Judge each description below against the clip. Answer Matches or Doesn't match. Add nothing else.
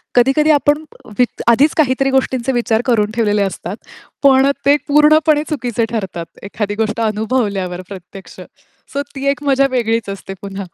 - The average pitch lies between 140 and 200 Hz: Doesn't match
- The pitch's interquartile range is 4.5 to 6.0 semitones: Matches